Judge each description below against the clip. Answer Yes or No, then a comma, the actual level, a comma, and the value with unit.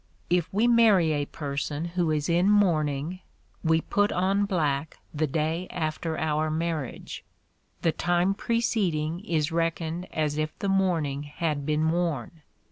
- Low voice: No, medium, 165 Hz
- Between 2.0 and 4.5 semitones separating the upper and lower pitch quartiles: Yes, average, 2.9 semitones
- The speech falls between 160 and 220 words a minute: No, average, 140 wpm